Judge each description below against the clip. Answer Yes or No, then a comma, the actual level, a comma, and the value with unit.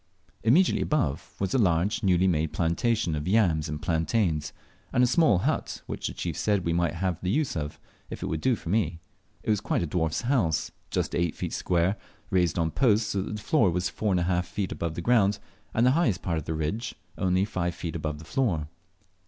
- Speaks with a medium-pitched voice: No, very low, 90 Hz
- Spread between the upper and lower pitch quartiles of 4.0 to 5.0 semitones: Yes, average, 4.7 semitones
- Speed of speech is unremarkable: No, fast, 220 wpm